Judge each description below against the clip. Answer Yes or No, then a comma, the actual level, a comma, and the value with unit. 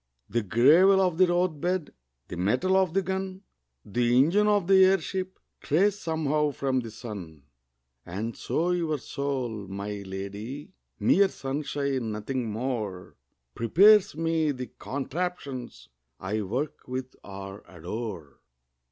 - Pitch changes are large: Yes, wide, 8.5 semitones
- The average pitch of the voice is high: No, low, 135 Hz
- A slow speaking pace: Yes, slow, 125 wpm